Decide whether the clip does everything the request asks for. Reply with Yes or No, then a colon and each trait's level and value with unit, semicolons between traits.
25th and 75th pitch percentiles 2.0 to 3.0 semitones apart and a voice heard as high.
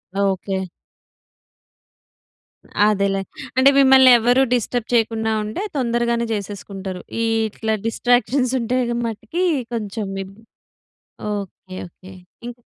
No: average, 3.5 semitones; high, 225 Hz